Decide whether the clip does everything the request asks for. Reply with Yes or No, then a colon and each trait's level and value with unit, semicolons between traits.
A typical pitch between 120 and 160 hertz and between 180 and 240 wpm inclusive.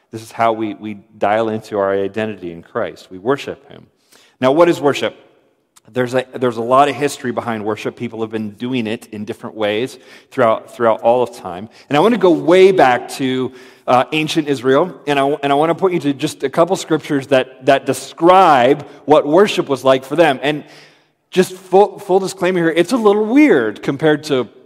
Yes: low, 135 Hz; fast, 205 wpm